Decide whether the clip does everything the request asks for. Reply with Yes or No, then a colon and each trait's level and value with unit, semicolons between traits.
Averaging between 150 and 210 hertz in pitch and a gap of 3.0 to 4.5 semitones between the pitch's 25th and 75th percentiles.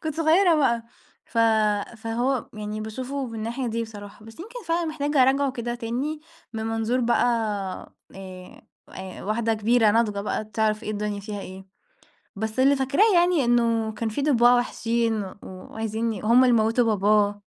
No: high, 230 Hz; average, 3.5 semitones